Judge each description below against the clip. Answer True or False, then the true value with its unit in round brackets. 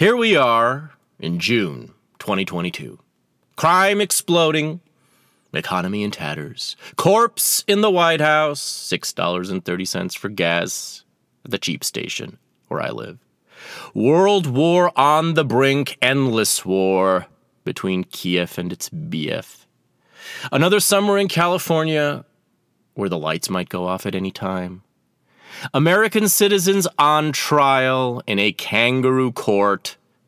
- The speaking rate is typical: False (115 wpm)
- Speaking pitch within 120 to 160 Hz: True (135 Hz)